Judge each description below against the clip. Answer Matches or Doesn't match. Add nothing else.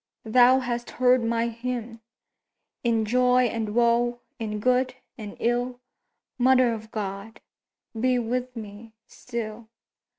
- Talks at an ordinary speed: Doesn't match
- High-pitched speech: Matches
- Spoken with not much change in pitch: Matches